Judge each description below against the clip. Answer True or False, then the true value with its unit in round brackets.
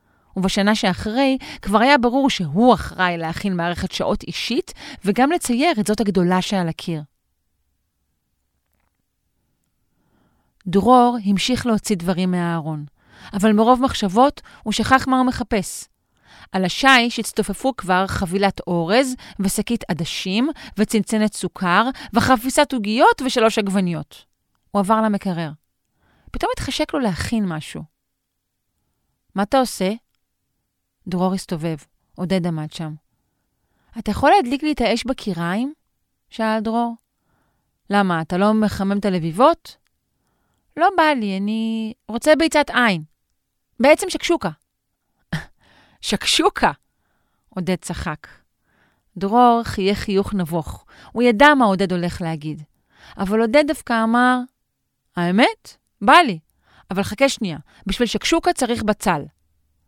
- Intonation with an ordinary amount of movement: False (5.9 semitones)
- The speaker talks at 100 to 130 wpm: True (110 wpm)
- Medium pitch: False (205 Hz)